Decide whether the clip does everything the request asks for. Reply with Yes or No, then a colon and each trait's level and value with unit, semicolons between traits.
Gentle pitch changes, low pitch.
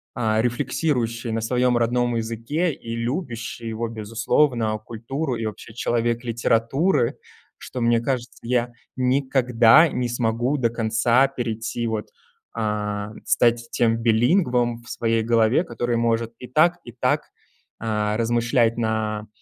Yes: narrow, 1.6 semitones; low, 115 Hz